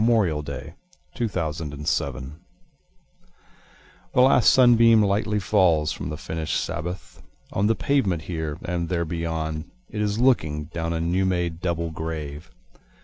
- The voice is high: No, very low, 85 Hz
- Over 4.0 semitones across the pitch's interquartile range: Yes, average, 4.6 semitones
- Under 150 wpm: Yes, slow, 135 wpm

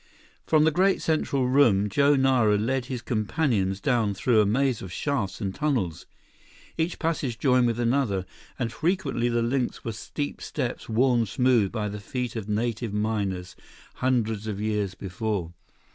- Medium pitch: No, low, 115 Hz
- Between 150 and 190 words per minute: Yes, average, 160 wpm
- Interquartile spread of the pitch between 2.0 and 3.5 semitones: No, average, 4.2 semitones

